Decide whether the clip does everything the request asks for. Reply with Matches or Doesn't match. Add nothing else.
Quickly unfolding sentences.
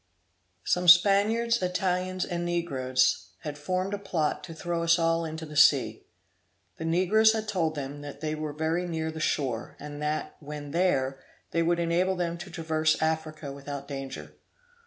Doesn't match